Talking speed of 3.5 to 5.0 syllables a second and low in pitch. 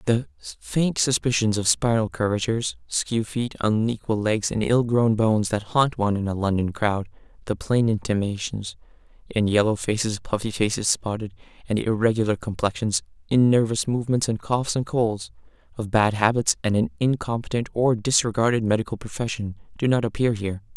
No: 5.3 syllables/s; low, 110 Hz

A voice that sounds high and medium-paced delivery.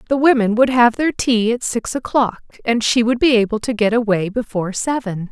No: high, 230 Hz; fast, 215 wpm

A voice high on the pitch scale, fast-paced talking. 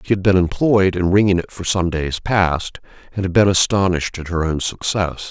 No: very low, 90 Hz; fast, 215 wpm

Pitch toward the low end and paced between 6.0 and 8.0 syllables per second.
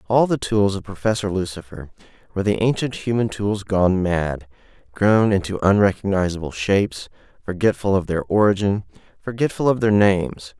No: low, 100 Hz; 5.2 syllables/s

